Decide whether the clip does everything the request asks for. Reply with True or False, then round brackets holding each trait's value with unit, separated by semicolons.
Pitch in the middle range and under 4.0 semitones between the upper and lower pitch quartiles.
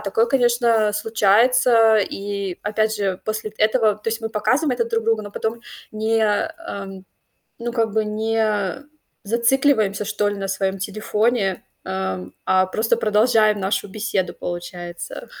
False (215 Hz; 2.4 semitones)